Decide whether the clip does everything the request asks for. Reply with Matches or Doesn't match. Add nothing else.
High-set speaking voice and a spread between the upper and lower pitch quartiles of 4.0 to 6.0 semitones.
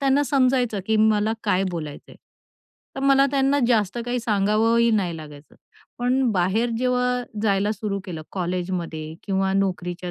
Matches